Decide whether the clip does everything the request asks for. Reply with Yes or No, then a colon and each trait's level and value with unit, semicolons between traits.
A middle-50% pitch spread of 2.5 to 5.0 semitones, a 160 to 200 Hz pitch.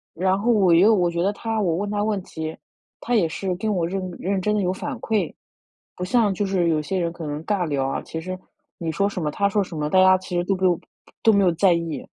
Yes: average, 3.1 semitones; medium, 185 Hz